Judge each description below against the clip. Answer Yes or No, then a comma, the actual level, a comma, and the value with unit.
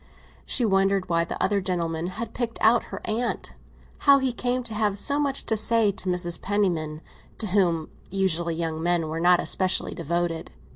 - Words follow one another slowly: No, average, 175 wpm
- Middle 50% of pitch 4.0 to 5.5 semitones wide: Yes, average, 4.6 semitones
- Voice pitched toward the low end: No, high, 190 Hz